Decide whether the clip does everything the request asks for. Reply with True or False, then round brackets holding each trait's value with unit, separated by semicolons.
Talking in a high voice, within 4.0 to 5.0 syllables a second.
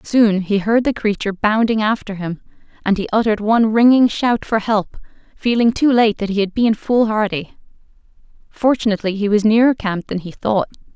False (215 Hz; 5.5 syllables/s)